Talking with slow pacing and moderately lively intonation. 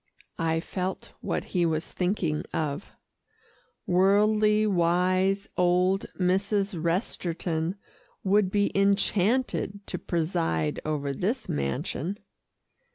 Yes: slow, 95 wpm; average, 3.4 semitones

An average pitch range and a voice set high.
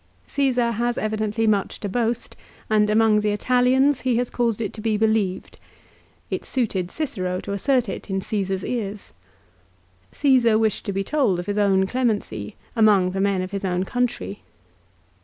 Yes: average, 3.7 semitones; high, 215 Hz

